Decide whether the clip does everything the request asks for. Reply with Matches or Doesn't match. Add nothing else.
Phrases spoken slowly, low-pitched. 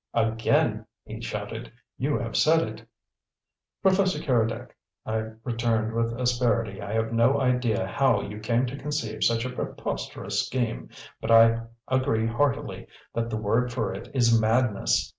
Doesn't match